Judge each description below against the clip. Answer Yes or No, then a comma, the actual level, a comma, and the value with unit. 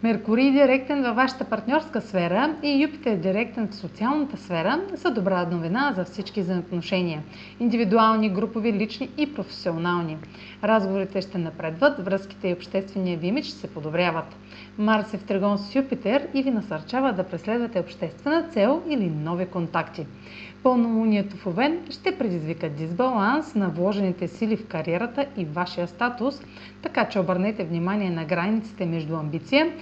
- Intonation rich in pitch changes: Yes, wide, 6.3 semitones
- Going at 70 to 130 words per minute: No, average, 145 wpm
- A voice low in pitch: No, high, 205 Hz